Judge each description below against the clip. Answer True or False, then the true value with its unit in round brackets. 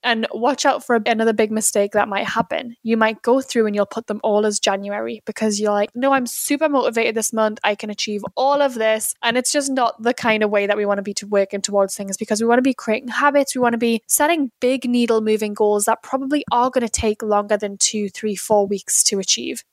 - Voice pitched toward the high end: True (220 Hz)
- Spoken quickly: True (240 wpm)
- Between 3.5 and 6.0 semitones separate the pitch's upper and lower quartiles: False (2.7 semitones)